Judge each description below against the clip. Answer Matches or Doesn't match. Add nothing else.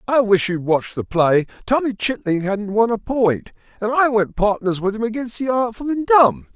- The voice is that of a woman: Doesn't match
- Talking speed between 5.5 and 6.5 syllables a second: Doesn't match